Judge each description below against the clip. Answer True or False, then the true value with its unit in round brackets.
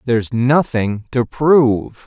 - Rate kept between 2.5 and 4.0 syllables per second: True (3.7 syllables/s)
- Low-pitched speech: True (125 Hz)